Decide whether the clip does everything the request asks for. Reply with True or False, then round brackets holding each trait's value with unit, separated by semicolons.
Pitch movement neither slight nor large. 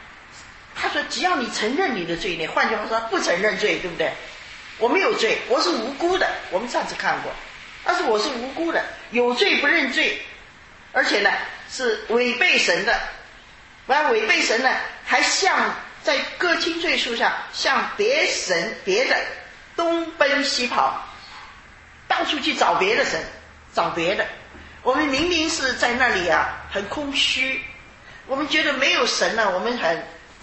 False (6.2 semitones)